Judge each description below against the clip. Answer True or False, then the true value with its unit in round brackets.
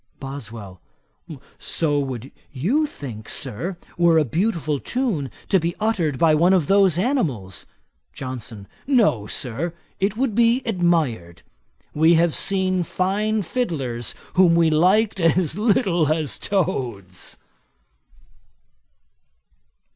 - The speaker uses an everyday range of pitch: False (6.8 semitones)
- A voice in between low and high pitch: True (165 Hz)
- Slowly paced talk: True (110 wpm)